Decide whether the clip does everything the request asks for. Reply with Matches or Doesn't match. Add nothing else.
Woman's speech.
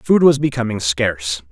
Doesn't match